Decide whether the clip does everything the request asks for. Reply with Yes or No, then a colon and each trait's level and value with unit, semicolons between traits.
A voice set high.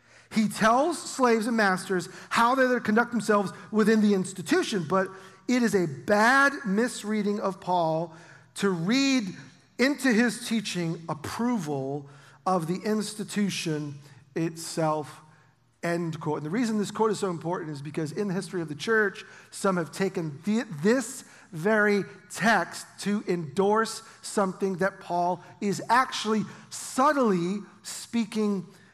Yes: high, 195 Hz